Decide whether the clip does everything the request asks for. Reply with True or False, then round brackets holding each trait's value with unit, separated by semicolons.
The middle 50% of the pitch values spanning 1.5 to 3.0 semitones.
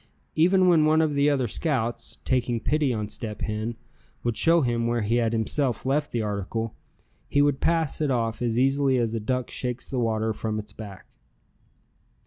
False (4.2 semitones)